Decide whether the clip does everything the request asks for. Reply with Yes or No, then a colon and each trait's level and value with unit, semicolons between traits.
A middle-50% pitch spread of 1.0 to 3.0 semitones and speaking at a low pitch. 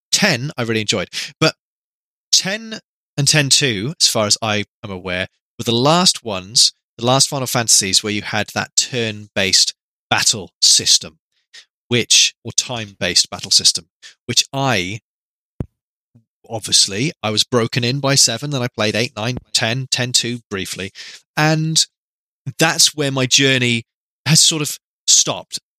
No: average, 4.8 semitones; low, 125 Hz